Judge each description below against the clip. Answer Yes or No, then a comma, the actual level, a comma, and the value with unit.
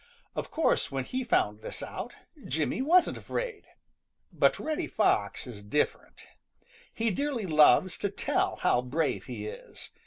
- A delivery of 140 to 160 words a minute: Yes, average, 145 wpm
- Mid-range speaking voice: Yes, medium, 165 Hz